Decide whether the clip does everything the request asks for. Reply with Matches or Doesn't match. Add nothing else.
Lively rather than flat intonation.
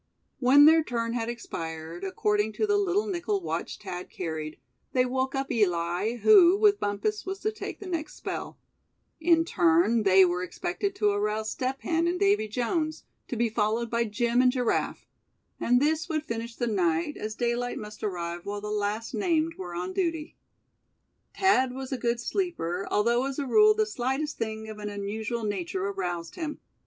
Matches